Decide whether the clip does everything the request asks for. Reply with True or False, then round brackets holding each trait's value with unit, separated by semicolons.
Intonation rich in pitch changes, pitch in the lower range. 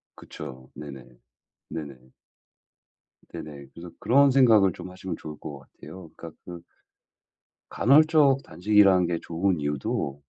True (6.4 semitones; 85 Hz)